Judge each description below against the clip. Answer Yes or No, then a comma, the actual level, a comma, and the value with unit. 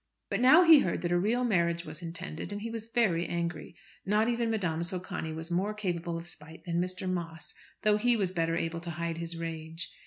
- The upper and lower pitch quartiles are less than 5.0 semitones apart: Yes, average, 4.0 semitones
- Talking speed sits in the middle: No, fast, 215 wpm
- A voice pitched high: No, medium, 175 Hz